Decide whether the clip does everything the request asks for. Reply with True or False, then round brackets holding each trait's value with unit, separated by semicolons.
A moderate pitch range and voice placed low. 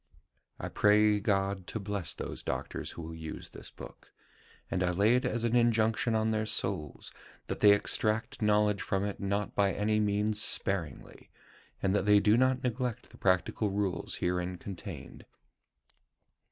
False (2.0 semitones; 105 Hz)